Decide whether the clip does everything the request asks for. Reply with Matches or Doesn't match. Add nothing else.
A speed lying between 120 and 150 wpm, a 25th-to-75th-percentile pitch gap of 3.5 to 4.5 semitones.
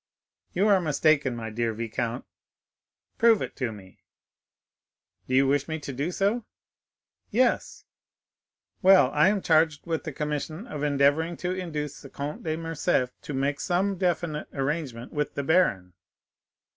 Matches